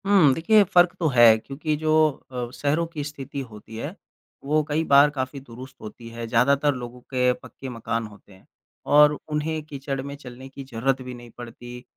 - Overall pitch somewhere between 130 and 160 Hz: Yes, low, 135 Hz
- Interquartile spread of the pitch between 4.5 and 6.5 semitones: No, average, 3.5 semitones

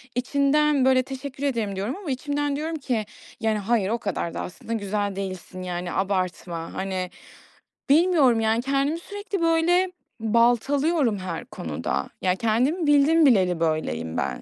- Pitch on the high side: Yes, high, 235 Hz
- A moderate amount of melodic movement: No, wide, 7.2 semitones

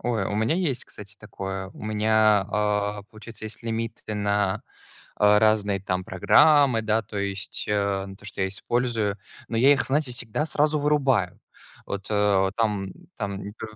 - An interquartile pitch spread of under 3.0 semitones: Yes, narrow, 2.4 semitones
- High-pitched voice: No, low, 105 Hz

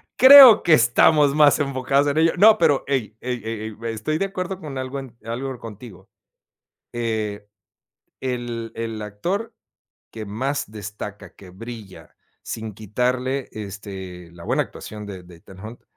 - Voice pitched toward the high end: No, low, 115 Hz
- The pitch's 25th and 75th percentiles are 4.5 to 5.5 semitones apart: Yes, average, 4.9 semitones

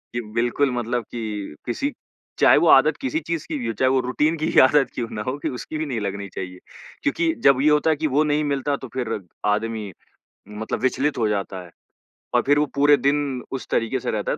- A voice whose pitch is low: Yes, low, 130 Hz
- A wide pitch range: No, average, 4.6 semitones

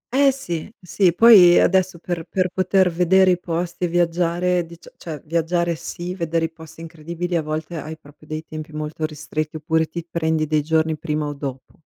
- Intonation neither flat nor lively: No, narrow, 2.2 semitones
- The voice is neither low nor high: Yes, medium, 165 Hz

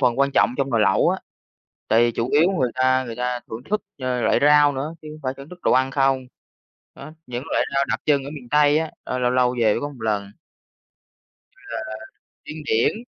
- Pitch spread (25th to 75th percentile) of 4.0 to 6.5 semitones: No, average, 2.9 semitones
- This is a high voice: No, low, 130 Hz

